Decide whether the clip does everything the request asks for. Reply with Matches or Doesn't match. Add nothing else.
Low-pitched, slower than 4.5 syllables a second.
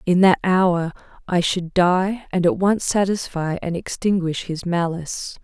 Doesn't match